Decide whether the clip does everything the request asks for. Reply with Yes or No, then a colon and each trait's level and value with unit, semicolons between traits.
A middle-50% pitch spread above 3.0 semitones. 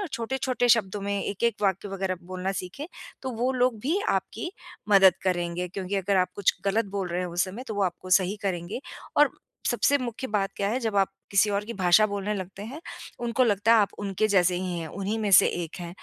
Yes: average, 3.4 semitones